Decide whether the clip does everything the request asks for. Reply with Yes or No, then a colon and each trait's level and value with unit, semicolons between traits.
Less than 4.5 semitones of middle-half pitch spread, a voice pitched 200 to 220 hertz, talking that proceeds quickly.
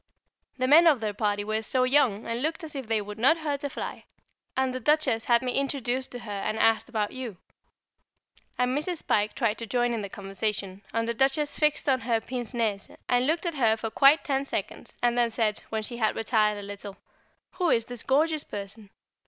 No: average, 4.0 semitones; high, 240 Hz; fast, 215 wpm